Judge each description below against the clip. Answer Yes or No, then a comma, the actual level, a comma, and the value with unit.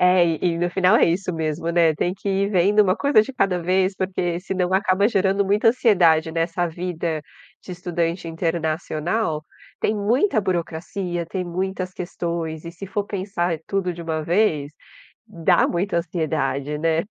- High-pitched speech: No, medium, 175 Hz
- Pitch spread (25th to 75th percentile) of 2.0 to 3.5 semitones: Yes, narrow, 2.6 semitones